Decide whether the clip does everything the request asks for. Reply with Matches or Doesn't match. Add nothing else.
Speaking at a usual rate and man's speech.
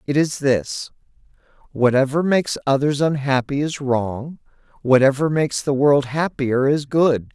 Doesn't match